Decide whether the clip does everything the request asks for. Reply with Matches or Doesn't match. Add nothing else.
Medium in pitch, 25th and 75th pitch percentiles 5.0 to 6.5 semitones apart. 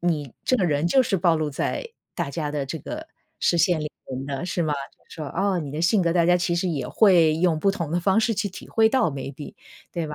Doesn't match